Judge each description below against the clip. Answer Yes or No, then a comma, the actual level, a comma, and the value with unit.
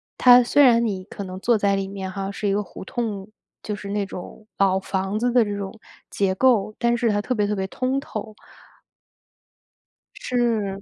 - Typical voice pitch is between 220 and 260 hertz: No, high, 205 Hz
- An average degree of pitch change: Yes, average, 3.3 semitones